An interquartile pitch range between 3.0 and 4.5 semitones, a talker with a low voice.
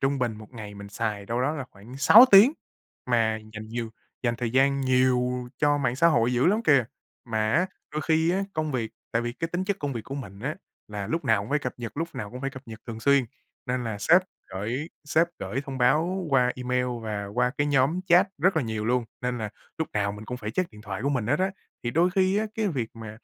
No: average, 5.0 semitones; low, 125 Hz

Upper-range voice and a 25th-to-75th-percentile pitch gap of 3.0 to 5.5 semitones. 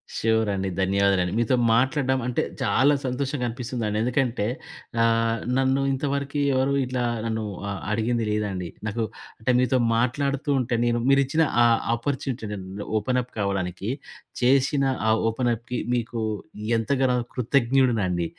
No: low, 120 Hz; average, 3.3 semitones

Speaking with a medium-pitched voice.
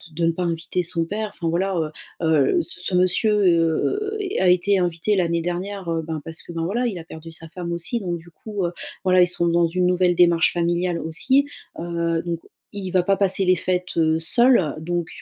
Yes: medium, 175 Hz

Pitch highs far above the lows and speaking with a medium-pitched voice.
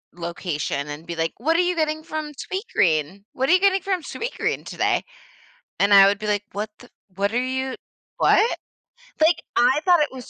No: wide, 9.0 semitones; very high, 255 Hz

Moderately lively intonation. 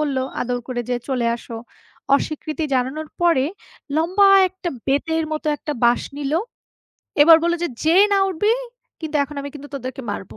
Yes: average, 4.0 semitones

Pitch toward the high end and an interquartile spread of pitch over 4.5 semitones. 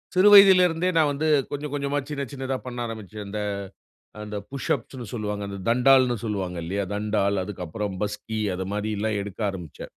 No: low, 110 Hz; average, 5.3 semitones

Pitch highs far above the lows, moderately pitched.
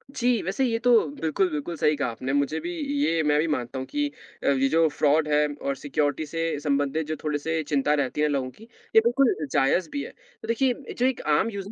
Yes: wide, 5.9 semitones; medium, 155 Hz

